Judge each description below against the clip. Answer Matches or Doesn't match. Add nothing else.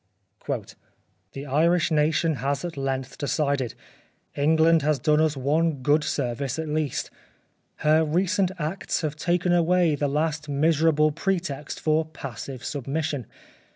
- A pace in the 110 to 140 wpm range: Matches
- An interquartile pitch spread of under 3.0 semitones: Matches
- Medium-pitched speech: Matches